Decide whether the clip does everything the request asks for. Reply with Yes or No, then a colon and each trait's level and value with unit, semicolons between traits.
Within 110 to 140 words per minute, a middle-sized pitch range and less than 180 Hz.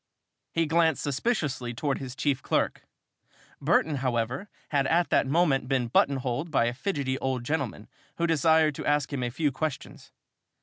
No: average, 165 wpm; average, 3.6 semitones; medium, 140 Hz